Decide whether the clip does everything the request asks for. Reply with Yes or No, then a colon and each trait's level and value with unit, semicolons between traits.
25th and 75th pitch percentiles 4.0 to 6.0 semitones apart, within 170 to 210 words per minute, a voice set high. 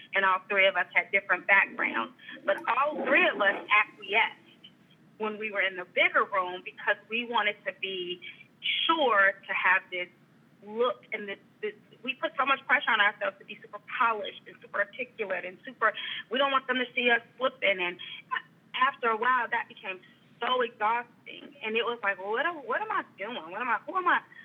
Yes: average, 4.8 semitones; average, 200 wpm; high, 220 Hz